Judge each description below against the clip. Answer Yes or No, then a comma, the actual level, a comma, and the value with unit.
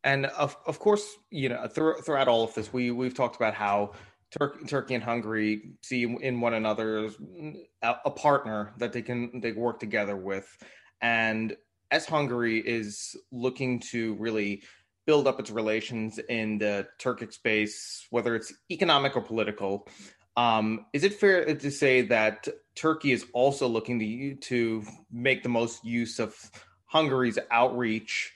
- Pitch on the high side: No, low, 120 Hz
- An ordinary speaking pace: No, fast, 155 wpm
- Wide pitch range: No, average, 3.5 semitones